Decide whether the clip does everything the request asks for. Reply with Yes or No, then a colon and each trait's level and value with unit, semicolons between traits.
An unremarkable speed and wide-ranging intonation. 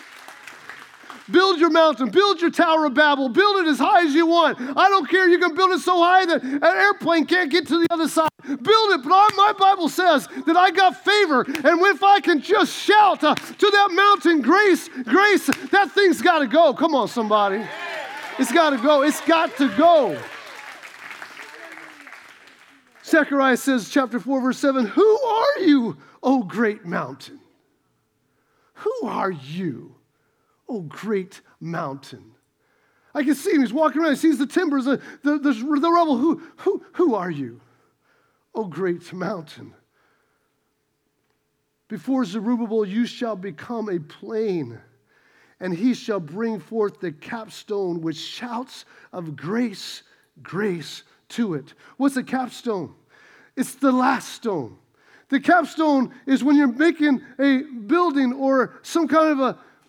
Yes: average, 155 wpm; wide, 7.4 semitones